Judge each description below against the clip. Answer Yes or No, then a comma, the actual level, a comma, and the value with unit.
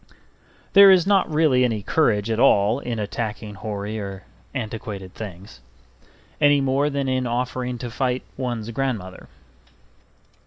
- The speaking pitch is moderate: No, low, 120 Hz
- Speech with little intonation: No, average, 4.4 semitones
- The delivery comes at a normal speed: No, slow, 130 wpm